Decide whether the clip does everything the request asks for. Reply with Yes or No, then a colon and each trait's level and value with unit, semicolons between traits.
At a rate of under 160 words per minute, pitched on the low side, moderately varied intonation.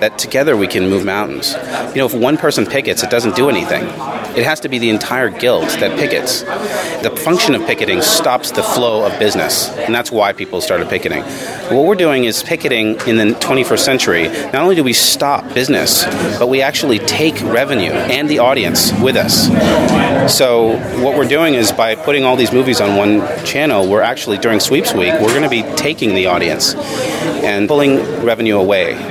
No: average, 190 wpm; low, 115 Hz; average, 3.6 semitones